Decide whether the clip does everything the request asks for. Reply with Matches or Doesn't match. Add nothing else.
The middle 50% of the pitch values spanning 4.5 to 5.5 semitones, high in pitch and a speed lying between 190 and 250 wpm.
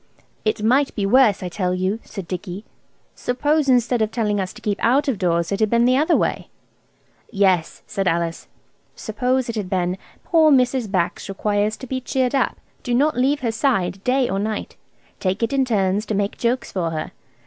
Matches